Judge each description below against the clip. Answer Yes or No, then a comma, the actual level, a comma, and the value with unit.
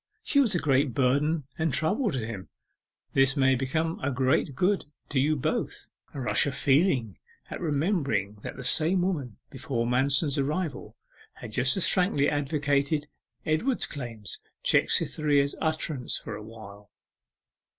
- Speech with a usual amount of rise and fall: Yes, average, 3.8 semitones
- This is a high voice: No, medium, 140 Hz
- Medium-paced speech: Yes, average, 145 wpm